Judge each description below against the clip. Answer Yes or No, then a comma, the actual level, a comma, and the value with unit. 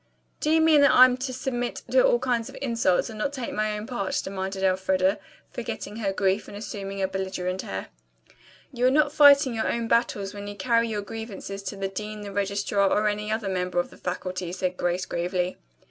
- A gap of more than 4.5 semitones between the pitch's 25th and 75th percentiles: No, average, 3.8 semitones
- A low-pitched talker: No, high, 205 Hz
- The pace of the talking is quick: Yes, fast, 210 wpm